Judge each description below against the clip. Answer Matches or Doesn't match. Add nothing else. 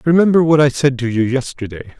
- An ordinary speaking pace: Doesn't match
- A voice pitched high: Doesn't match